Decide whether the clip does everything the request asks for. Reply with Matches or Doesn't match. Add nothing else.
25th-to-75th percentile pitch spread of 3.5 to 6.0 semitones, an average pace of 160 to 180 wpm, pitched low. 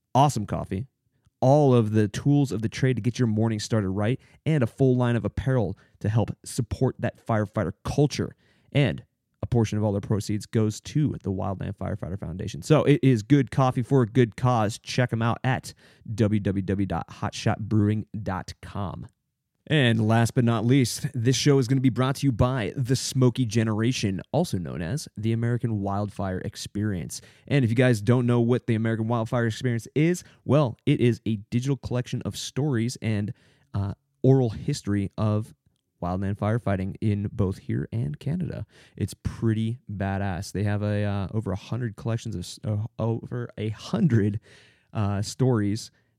Matches